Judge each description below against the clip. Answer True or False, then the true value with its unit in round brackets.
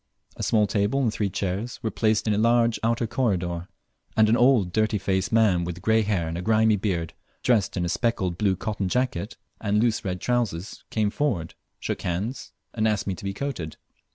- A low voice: True (105 Hz)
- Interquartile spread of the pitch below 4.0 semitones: True (3.6 semitones)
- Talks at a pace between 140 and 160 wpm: False (200 wpm)